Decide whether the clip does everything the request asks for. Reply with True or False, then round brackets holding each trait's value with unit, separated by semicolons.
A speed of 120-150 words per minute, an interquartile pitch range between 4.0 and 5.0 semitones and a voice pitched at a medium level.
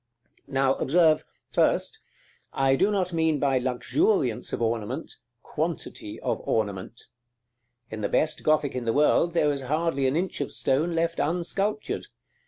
True (145 wpm; 4.5 semitones; 145 Hz)